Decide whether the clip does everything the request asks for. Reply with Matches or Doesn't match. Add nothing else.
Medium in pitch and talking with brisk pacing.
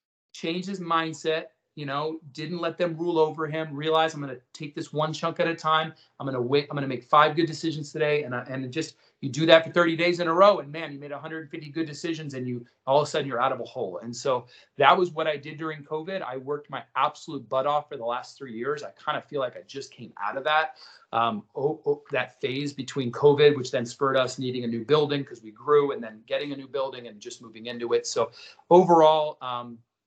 Matches